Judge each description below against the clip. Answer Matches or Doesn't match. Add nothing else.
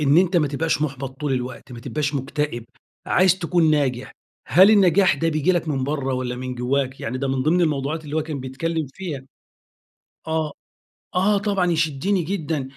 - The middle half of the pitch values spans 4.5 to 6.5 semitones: Doesn't match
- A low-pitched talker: Doesn't match